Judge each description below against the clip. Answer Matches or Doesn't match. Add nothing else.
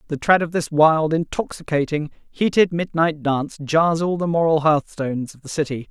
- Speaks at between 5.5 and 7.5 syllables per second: Doesn't match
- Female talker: Doesn't match